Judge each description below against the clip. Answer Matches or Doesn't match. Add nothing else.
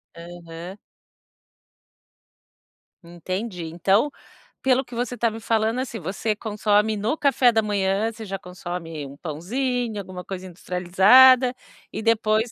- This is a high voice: Matches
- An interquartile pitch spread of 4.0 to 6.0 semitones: Matches